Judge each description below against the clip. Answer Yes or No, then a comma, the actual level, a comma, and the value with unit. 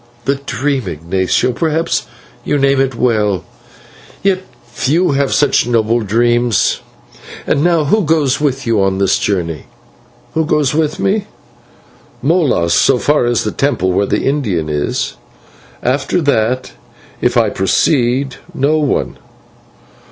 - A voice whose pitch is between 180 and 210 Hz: No, low, 130 Hz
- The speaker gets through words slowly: Yes, slow, 130 wpm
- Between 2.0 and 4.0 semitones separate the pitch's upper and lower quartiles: No, wide, 5.4 semitones